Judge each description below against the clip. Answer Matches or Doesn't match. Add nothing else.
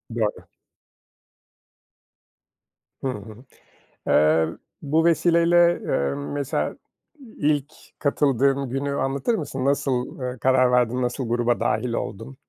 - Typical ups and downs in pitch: Matches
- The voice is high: Doesn't match